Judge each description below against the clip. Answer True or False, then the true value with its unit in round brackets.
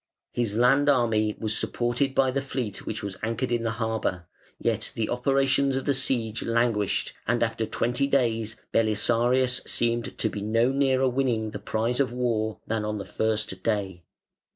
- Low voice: True (115 Hz)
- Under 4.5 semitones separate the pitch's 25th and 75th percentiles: True (2.8 semitones)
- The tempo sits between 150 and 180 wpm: True (170 wpm)